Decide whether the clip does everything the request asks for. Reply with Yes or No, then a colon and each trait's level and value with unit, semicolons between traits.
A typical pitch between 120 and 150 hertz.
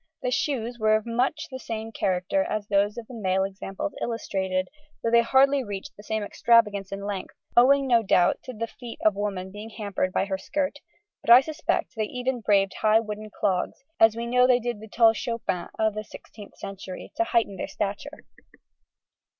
No: high, 220 Hz